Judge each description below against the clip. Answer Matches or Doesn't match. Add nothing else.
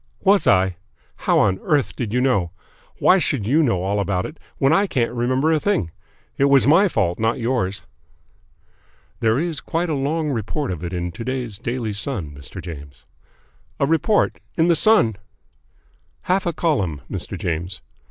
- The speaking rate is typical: Matches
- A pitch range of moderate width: Doesn't match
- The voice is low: Matches